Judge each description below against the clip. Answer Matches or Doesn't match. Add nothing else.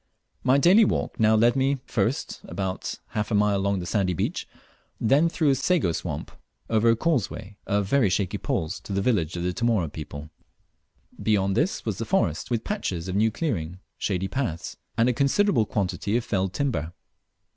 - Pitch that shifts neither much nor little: Doesn't match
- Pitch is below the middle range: Matches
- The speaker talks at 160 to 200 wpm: Matches